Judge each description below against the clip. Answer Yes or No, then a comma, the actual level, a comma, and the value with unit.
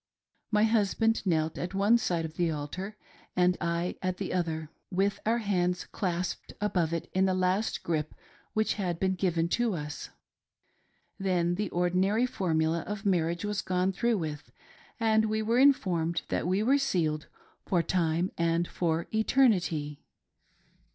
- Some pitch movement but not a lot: Yes, average, 3.7 semitones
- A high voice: No, medium, 180 Hz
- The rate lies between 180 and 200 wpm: No, average, 150 wpm